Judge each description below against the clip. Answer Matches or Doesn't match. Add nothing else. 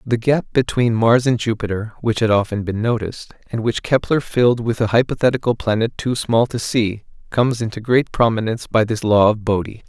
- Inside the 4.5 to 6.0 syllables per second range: Matches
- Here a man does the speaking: Matches